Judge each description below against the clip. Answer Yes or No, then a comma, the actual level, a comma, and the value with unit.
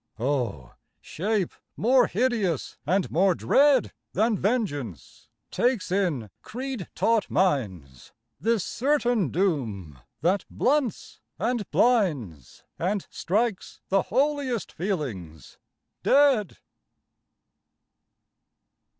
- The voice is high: Yes, high, 195 Hz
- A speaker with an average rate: No, slow, 85 wpm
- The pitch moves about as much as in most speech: No, wide, 8.9 semitones